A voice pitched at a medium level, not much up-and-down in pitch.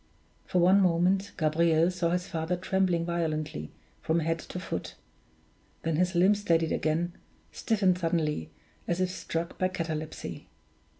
Yes: medium, 170 Hz; narrow, 2.2 semitones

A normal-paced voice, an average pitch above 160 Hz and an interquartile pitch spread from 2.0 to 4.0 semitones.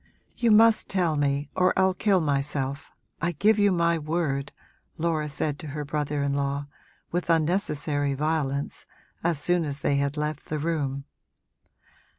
No: average, 155 wpm; medium, 150 Hz; average, 3.3 semitones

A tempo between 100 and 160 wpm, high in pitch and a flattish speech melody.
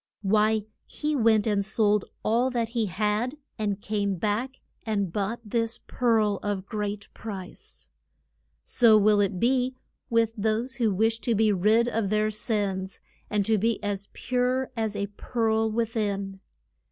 Yes: average, 155 wpm; high, 215 Hz; narrow, 2.1 semitones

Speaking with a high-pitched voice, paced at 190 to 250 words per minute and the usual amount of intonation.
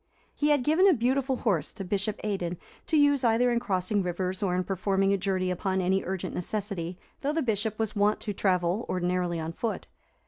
Yes: high, 195 Hz; average, 200 wpm; average, 4.1 semitones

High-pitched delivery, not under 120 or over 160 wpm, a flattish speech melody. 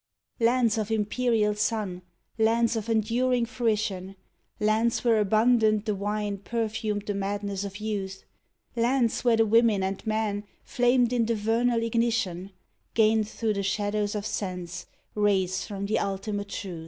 Yes: high, 215 Hz; average, 150 wpm; narrow, 2.2 semitones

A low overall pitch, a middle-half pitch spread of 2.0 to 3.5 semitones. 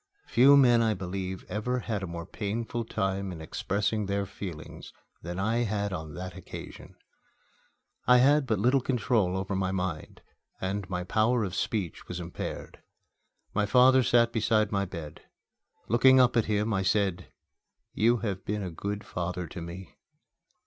No: low, 100 Hz; average, 4.0 semitones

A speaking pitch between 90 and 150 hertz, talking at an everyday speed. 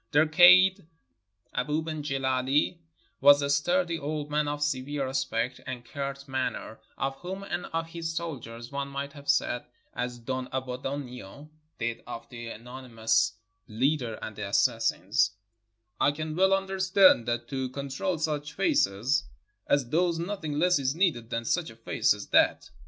Yes: medium, 140 Hz; average, 155 wpm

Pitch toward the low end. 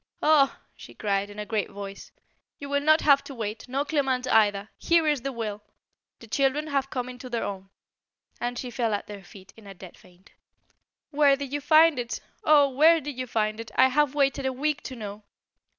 No: very high, 255 Hz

